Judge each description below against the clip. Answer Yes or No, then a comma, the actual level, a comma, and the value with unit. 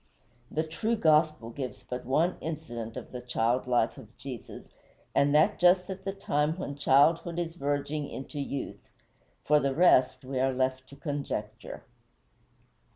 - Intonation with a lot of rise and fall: No, average, 3.9 semitones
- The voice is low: No, medium, 145 Hz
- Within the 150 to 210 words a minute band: Yes, average, 155 wpm